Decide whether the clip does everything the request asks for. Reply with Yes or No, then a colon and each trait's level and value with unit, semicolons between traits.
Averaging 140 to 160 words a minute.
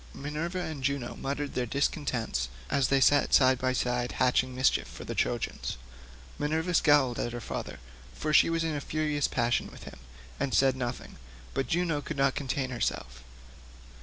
No: average, 170 wpm